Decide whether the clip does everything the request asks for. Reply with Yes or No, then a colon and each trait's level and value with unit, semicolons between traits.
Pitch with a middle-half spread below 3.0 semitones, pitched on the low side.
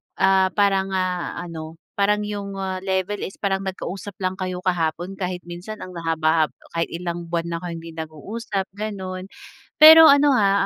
No: narrow, 2.6 semitones; medium, 185 Hz